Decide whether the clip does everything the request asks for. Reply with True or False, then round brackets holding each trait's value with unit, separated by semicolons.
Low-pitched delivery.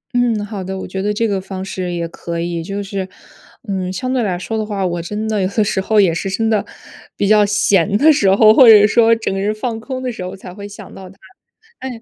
False (200 Hz)